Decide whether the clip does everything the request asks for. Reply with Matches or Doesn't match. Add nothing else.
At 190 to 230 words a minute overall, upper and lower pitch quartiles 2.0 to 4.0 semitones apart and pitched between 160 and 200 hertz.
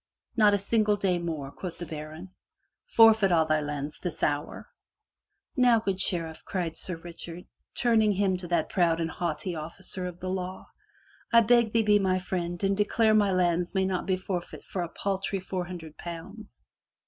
Matches